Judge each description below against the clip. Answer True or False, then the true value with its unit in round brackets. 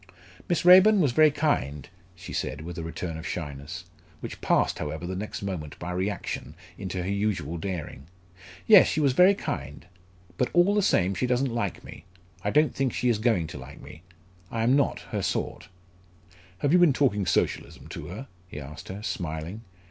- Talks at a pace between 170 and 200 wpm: True (185 wpm)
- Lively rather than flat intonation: True (8.4 semitones)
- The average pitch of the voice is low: True (100 Hz)